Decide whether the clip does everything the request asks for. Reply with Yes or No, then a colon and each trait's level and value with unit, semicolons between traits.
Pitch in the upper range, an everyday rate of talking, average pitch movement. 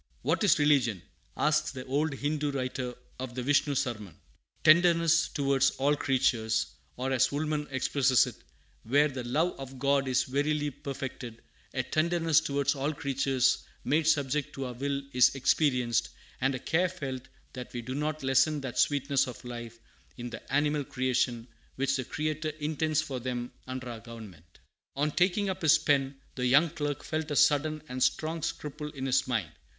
No: medium, 140 Hz; average, 170 wpm; average, 3.0 semitones